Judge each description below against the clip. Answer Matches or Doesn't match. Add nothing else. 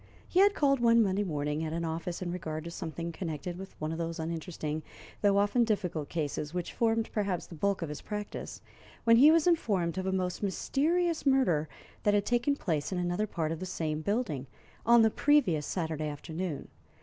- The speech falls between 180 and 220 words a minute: Matches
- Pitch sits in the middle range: Matches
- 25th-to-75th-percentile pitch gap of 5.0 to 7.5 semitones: Matches